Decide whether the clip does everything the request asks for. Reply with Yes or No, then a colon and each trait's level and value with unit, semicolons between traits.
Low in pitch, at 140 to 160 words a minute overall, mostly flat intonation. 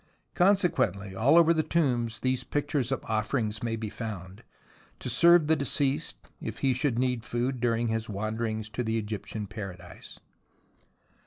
No: low, 115 Hz; average, 150 wpm; average, 4.1 semitones